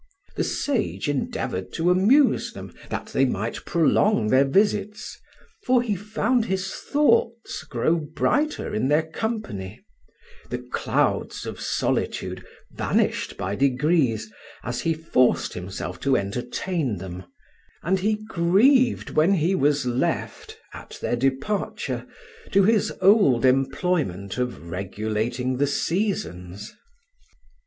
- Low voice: No, medium, 150 Hz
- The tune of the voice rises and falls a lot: Yes, wide, 8.8 semitones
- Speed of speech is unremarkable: No, slow, 115 wpm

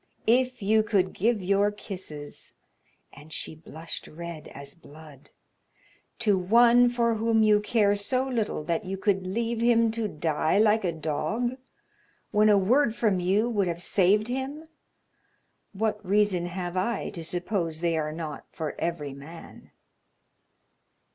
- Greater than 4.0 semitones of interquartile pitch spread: Yes, average, 5.0 semitones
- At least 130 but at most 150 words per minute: Yes, average, 145 wpm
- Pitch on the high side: Yes, high, 200 Hz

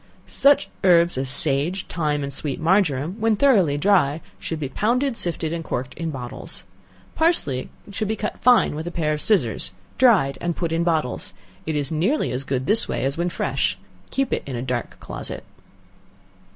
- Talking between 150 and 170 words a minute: No, average, 180 wpm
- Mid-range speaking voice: Yes, medium, 165 Hz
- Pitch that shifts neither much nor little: No, wide, 6.5 semitones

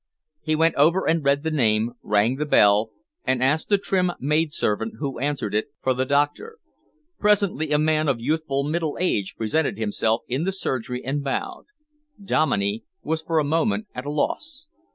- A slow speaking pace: No, average, 175 wpm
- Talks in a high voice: No, medium, 145 Hz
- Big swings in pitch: No, average, 4.3 semitones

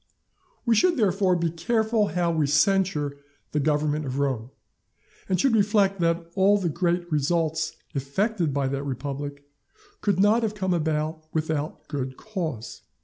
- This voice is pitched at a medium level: Yes, medium, 165 Hz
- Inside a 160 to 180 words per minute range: No, average, 145 wpm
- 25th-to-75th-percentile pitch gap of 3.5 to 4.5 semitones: No, average, 5.2 semitones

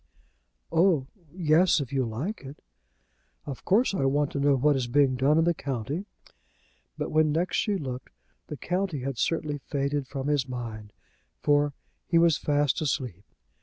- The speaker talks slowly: No, average, 165 wpm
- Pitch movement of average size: Yes, average, 3.3 semitones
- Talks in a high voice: No, medium, 145 Hz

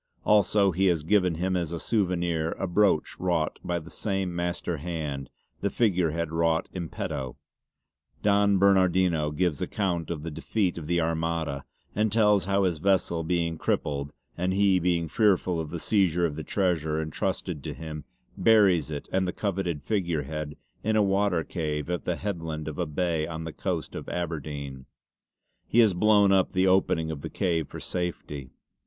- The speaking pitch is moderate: No, very low, 85 Hz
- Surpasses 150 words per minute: Yes, average, 175 wpm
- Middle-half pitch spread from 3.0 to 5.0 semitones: Yes, average, 3.4 semitones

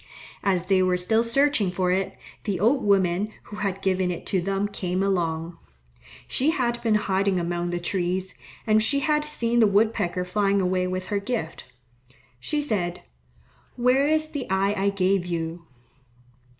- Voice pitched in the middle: No, high, 195 Hz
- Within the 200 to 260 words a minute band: No, average, 165 wpm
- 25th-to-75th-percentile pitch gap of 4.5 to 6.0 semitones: No, average, 3.6 semitones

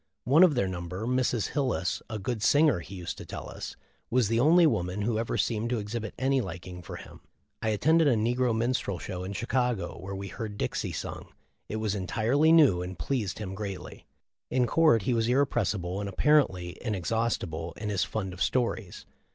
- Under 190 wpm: No, average, 195 wpm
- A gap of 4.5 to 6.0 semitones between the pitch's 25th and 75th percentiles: Yes, average, 4.8 semitones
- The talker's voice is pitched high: No, low, 110 Hz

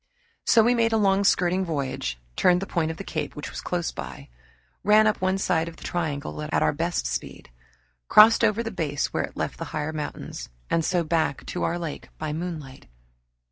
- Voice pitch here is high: No, medium, 170 Hz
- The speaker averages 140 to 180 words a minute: No, fast, 205 wpm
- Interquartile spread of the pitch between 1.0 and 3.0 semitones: No, average, 4.2 semitones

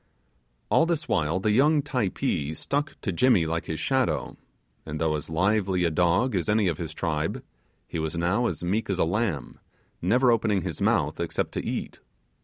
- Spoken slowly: No, average, 185 wpm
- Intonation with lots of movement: Yes, wide, 6.2 semitones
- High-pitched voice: No, very low, 95 Hz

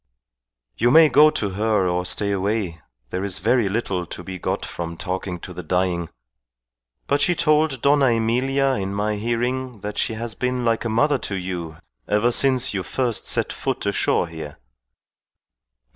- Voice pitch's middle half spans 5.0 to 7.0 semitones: Yes, wide, 5.4 semitones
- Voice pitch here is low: Yes, low, 105 Hz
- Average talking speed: Yes, average, 170 wpm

